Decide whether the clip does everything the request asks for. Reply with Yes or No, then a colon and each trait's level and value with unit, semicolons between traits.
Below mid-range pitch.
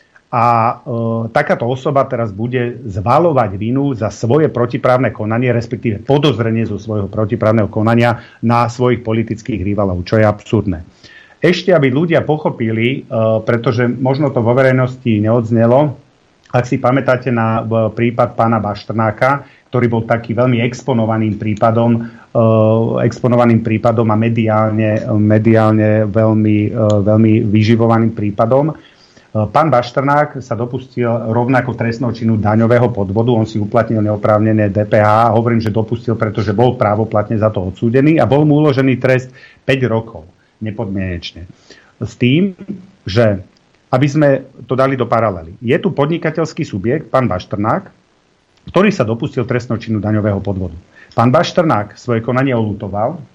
Yes: low, 115 Hz